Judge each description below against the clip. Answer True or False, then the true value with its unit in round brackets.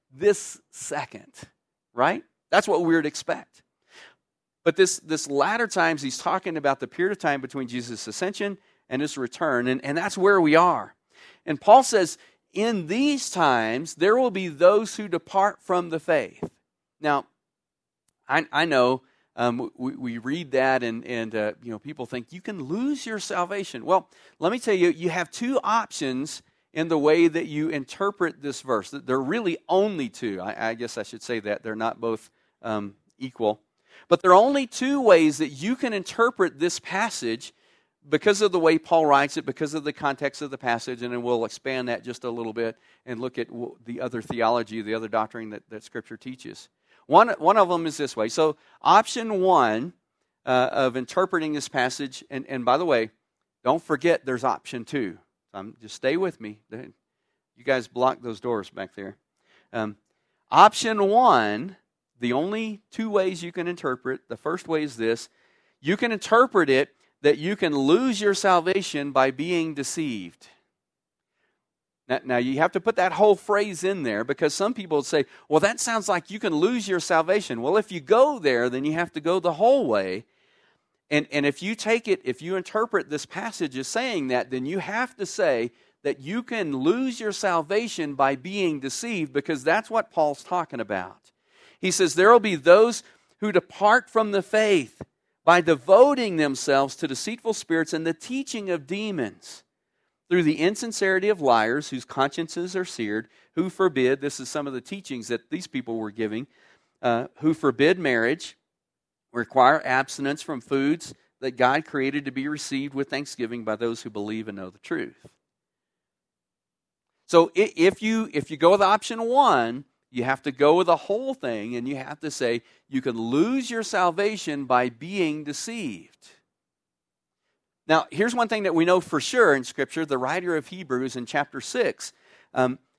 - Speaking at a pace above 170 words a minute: True (180 wpm)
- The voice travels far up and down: True (7.2 semitones)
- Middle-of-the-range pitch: True (155 Hz)